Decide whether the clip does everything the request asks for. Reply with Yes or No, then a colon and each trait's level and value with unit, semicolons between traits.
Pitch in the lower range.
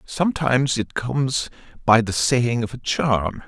Yes: low, 125 Hz